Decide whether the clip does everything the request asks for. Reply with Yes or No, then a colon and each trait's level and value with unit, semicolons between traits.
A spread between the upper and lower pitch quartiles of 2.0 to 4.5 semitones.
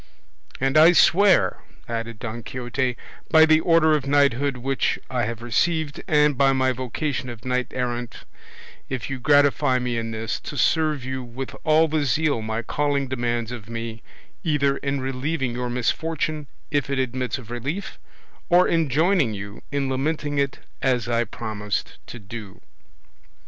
Yes: average, 3.7 semitones